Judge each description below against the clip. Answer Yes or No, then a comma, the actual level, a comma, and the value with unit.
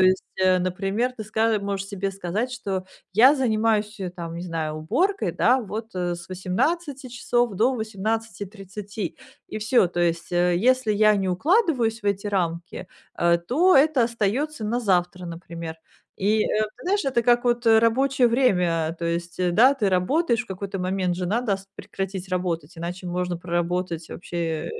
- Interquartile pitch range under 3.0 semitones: No, average, 4.8 semitones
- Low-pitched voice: No, high, 200 Hz